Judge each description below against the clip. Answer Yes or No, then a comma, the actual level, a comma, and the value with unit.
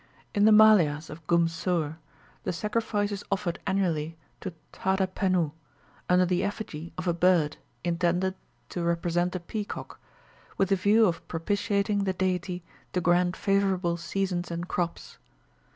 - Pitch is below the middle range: No, medium, 180 Hz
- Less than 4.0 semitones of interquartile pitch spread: Yes, narrow, 2.6 semitones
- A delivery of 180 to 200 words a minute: No, average, 140 wpm